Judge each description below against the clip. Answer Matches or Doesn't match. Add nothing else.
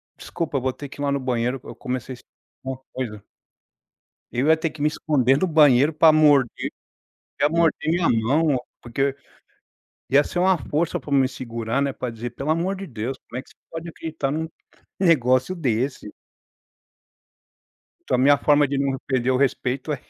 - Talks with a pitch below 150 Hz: Matches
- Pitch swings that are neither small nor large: Matches